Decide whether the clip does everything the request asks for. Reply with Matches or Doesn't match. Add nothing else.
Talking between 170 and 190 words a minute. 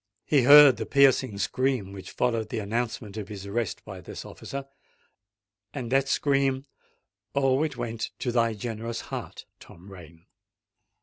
Doesn't match